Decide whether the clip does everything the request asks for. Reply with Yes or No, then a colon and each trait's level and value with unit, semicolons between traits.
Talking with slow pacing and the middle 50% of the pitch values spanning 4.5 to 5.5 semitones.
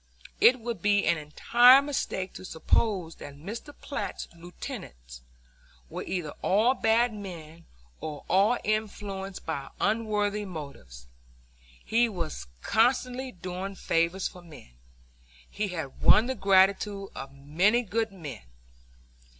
Yes: slow, 120 wpm; average, 5.2 semitones